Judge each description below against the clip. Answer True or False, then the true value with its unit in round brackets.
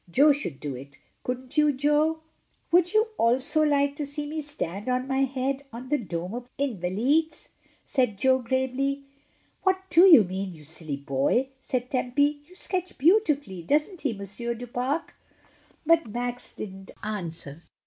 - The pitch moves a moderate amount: False (6.2 semitones)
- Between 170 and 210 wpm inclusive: False (160 wpm)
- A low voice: False (260 Hz)